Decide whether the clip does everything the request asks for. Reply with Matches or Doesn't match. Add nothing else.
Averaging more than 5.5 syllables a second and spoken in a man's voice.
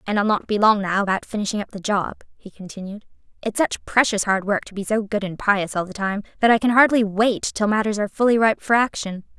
Doesn't match